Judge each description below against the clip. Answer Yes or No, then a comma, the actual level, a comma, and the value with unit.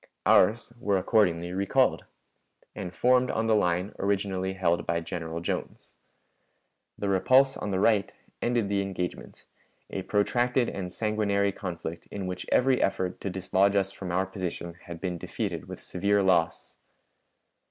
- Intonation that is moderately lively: No, narrow, 2.3 semitones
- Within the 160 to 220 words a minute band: No, average, 145 wpm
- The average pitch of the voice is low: Yes, very low, 95 Hz